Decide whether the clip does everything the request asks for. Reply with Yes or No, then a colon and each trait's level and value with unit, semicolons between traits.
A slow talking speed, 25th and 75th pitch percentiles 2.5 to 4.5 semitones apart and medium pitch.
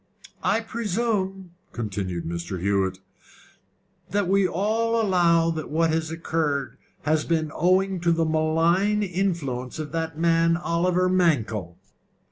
Yes: slow, 120 wpm; average, 3.6 semitones; medium, 165 Hz